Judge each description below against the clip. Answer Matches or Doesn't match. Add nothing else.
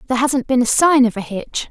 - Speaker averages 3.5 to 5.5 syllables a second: Doesn't match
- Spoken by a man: Doesn't match